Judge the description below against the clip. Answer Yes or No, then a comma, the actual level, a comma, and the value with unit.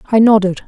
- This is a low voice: No, high, 210 Hz